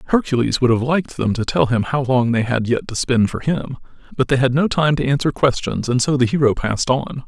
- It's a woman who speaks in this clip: No, male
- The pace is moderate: No, fast, 255 wpm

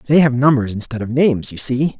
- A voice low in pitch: Yes, low, 130 Hz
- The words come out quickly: Yes, fast, 240 wpm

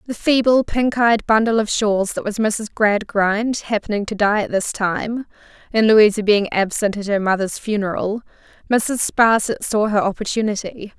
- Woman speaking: Yes, female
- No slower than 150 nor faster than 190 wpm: Yes, average, 165 wpm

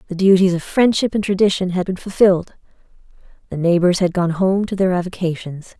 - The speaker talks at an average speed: Yes, average, 175 wpm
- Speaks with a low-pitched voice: No, medium, 185 Hz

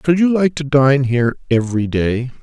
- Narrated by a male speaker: Yes, male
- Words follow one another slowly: No, average, 200 wpm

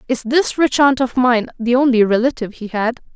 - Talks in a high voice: Yes, high, 245 Hz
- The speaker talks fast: Yes, fast, 210 wpm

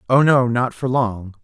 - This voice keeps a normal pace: No, fast, 210 wpm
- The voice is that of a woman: No, male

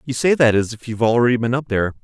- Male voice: Yes, male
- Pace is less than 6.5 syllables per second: No, 7.6 syllables/s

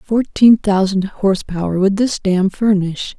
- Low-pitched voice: No, high, 200 Hz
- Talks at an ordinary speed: No, slow, 130 wpm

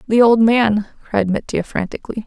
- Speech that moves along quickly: No, average, 160 wpm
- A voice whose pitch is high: Yes, high, 220 Hz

